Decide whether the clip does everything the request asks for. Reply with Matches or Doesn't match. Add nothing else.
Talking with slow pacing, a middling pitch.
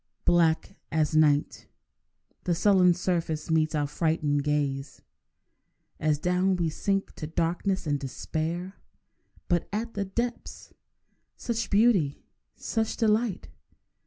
Matches